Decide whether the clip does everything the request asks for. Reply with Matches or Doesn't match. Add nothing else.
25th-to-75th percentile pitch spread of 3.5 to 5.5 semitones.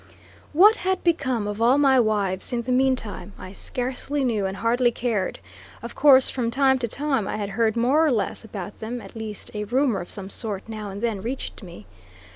Matches